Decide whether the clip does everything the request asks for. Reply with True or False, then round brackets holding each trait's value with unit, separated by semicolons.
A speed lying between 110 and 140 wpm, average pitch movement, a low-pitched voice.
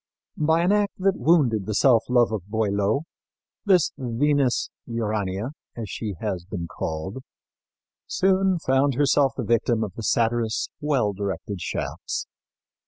False (135 wpm; 5.7 semitones; 115 Hz)